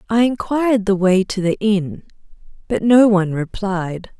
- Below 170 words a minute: Yes, average, 155 wpm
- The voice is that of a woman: Yes, female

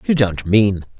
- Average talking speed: Yes, average, 180 wpm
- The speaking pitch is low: Yes, low, 110 Hz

